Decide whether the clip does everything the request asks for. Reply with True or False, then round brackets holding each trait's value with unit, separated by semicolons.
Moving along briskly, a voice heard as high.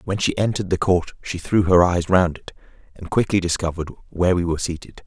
False (215 wpm; 90 Hz)